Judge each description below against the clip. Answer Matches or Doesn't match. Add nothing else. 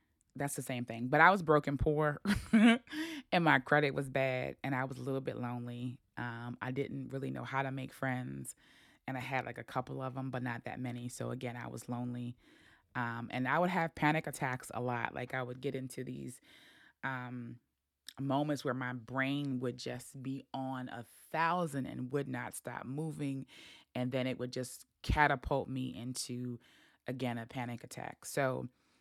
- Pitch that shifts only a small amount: Matches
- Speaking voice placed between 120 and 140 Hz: Matches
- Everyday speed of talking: Matches